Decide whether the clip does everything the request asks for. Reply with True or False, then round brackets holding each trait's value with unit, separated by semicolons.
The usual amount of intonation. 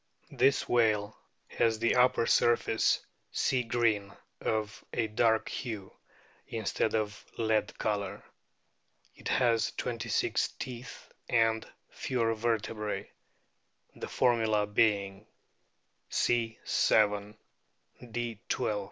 False (1.8 semitones)